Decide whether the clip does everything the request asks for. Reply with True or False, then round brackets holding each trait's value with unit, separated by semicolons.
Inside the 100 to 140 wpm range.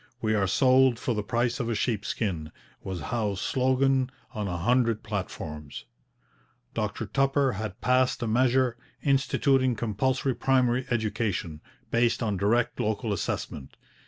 True (135 wpm)